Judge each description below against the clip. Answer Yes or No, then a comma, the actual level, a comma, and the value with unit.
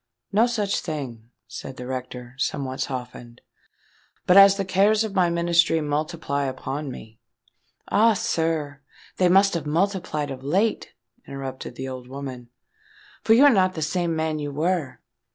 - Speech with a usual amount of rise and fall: No, wide, 6.0 semitones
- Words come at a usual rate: Yes, average, 150 wpm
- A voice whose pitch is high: No, medium, 155 Hz